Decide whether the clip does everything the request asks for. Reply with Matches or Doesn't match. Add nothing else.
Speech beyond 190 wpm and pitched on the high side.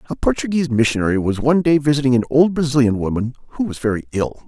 Doesn't match